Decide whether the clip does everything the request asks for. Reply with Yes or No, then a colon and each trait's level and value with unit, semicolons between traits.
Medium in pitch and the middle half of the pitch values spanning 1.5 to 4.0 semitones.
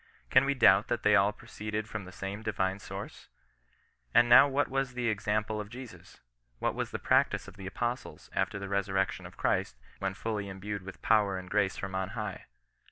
No: low, 105 Hz; average, 2.7 semitones